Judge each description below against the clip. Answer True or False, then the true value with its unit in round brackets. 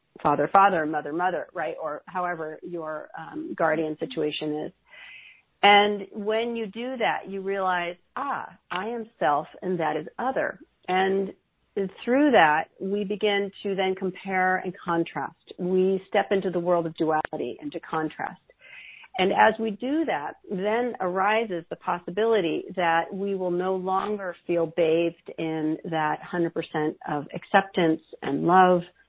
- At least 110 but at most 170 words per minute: True (145 wpm)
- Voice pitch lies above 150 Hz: True (185 Hz)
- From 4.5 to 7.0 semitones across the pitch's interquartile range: False (3.4 semitones)